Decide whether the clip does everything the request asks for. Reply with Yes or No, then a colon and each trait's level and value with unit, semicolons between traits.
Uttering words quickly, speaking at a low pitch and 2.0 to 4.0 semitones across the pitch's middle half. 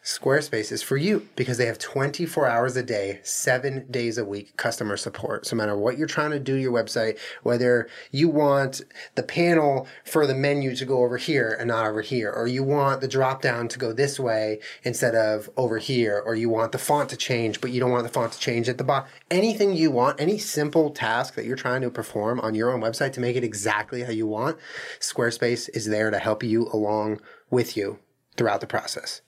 Yes: fast, 225 wpm; low, 125 Hz; average, 3.6 semitones